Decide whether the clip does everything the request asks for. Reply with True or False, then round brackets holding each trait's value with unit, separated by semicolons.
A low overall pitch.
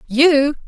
False (285 Hz)